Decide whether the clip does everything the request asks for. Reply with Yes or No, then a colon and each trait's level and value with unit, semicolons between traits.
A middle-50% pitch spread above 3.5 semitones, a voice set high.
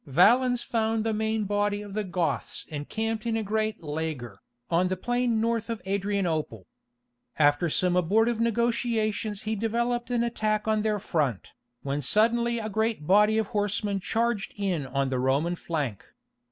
Yes: average, 4.9 semitones; high, 210 Hz